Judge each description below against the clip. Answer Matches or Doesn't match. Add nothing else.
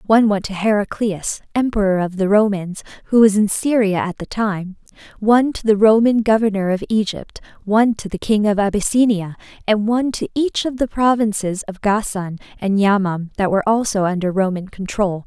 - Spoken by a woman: Matches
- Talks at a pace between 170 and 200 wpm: Matches